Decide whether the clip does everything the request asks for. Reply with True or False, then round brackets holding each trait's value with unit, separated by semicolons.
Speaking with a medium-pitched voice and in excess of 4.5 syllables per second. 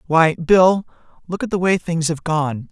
False (170 Hz; 4.3 syllables/s)